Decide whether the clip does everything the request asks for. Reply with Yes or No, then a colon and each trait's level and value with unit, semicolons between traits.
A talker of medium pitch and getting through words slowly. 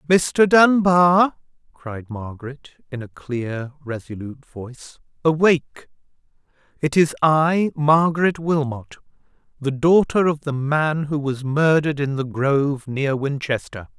Yes: medium, 145 Hz; slow, 120 wpm